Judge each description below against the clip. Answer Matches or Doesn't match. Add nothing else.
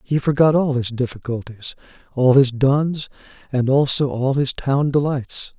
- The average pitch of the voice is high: Doesn't match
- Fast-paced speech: Doesn't match